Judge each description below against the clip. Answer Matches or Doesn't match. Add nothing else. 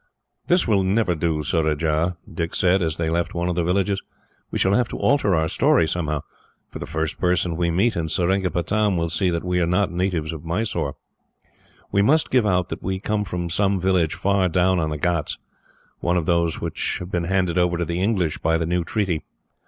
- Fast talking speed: Matches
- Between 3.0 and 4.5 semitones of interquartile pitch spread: Doesn't match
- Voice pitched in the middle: Doesn't match